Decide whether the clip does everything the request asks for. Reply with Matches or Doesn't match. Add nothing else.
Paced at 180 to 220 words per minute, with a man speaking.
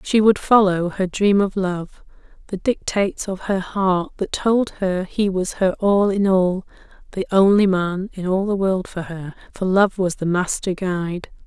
Doesn't match